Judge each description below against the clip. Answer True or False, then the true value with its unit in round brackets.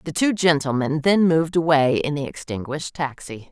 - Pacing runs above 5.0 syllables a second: True (5.4 syllables/s)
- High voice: False (150 Hz)